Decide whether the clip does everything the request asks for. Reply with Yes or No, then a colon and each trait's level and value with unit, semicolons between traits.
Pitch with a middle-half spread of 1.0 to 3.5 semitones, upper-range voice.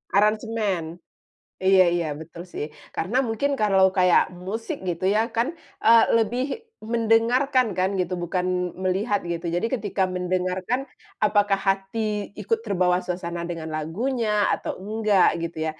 No: average, 3.9 semitones; high, 195 Hz